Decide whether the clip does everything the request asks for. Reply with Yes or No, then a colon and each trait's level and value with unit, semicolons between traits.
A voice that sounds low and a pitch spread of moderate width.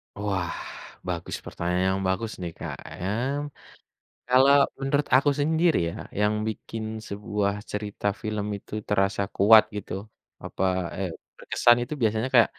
Yes: low, 105 Hz; average, 3.7 semitones